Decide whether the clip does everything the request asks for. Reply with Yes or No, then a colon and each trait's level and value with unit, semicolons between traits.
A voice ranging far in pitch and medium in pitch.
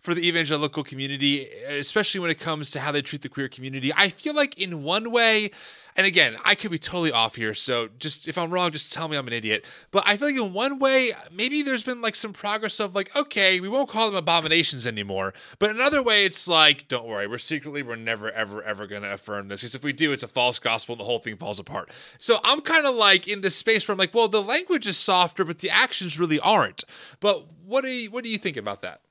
Yes: wide, 7.7 semitones; medium, 175 Hz